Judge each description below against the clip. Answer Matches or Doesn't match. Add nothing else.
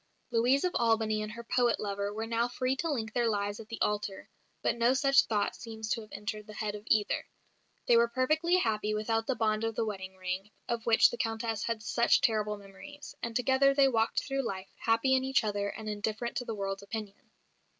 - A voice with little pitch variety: Matches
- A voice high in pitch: Matches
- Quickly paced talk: Matches